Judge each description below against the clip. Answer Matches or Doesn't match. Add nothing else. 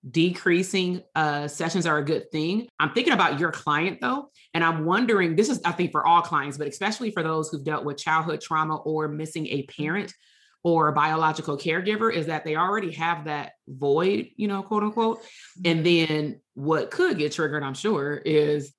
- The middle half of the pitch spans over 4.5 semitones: Doesn't match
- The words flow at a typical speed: Matches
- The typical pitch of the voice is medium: Matches